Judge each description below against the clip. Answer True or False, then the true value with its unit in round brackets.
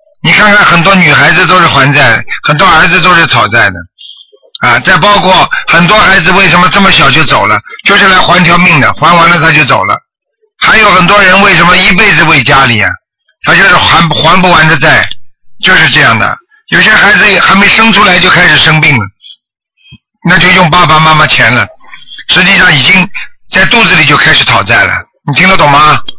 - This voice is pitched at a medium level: True (180 Hz)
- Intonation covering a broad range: False (4.2 semitones)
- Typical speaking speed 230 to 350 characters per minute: True (285 characters per minute)